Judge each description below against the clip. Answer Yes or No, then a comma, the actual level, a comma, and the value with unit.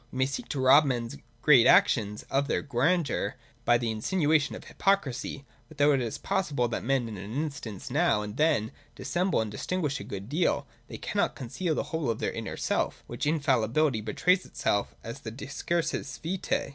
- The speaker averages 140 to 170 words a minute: No, average, 195 wpm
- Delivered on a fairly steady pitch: No, average, 5.3 semitones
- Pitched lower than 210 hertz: Yes, medium, 140 Hz